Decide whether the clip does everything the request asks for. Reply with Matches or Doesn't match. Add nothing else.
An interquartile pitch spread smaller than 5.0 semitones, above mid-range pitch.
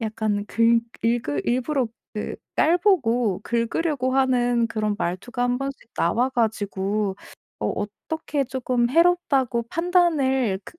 Matches